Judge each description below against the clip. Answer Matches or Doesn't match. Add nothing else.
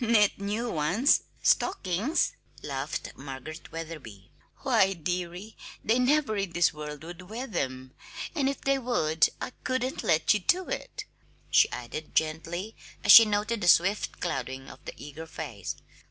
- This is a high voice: Doesn't match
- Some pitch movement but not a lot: Doesn't match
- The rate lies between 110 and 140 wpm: Doesn't match